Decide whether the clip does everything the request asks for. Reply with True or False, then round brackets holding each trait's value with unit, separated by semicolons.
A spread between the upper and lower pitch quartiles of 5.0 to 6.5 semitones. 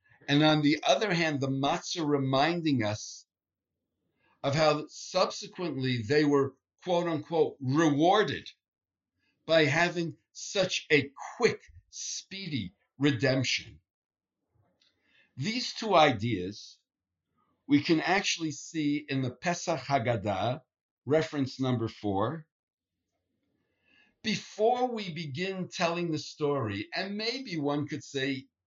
True (5.6 semitones)